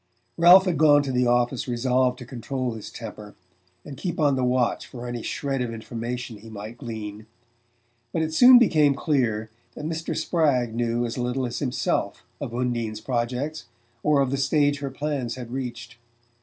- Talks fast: No, average, 175 wpm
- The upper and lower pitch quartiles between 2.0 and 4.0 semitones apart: Yes, average, 3.4 semitones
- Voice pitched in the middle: No, low, 125 Hz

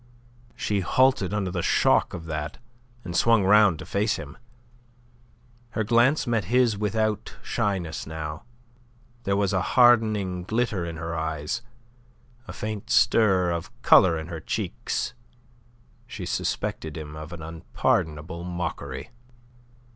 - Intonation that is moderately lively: Yes, average, 4.9 semitones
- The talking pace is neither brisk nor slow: No, slow, 130 wpm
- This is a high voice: No, very low, 90 Hz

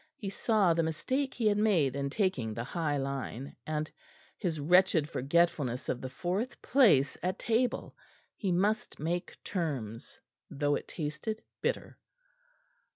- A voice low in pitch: No, medium, 165 Hz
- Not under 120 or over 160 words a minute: Yes, average, 140 wpm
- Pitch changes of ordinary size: No, wide, 6.3 semitones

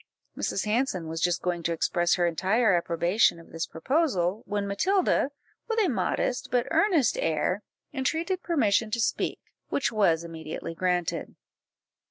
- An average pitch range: No, wide, 6.9 semitones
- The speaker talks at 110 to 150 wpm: Yes, average, 145 wpm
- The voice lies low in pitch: No, high, 195 Hz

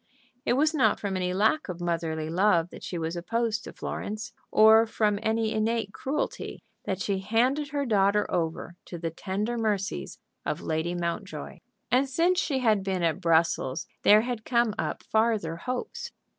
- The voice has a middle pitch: No, high, 210 Hz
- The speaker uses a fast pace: No, average, 170 wpm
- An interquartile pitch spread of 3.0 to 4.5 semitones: No, average, 4.9 semitones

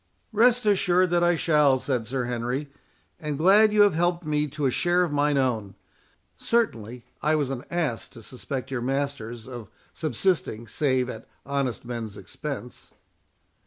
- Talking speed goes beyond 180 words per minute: No, average, 160 wpm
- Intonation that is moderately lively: No, wide, 5.9 semitones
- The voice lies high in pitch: No, medium, 140 Hz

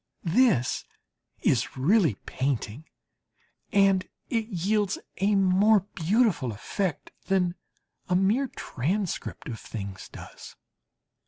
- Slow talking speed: Yes, slow, 95 wpm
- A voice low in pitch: No, high, 190 Hz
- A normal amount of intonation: No, wide, 6.5 semitones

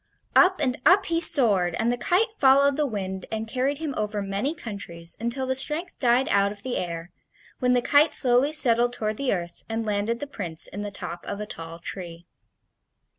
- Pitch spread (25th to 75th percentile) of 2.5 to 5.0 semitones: No, wide, 5.6 semitones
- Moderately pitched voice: No, high, 235 Hz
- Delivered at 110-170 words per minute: No, average, 200 wpm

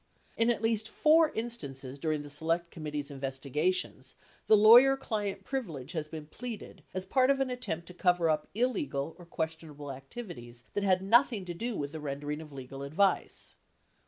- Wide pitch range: Yes, wide, 7.2 semitones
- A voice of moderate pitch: Yes, medium, 170 Hz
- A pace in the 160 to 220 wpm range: Yes, average, 180 wpm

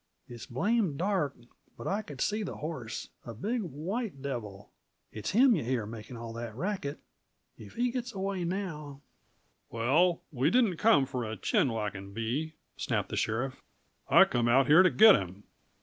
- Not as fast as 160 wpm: No, average, 175 wpm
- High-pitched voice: No, medium, 145 Hz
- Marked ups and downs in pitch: Yes, wide, 8.6 semitones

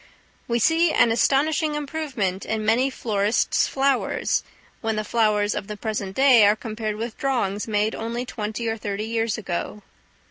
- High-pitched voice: Yes, high, 225 Hz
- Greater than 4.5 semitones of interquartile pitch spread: No, average, 3.3 semitones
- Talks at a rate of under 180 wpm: Yes, average, 155 wpm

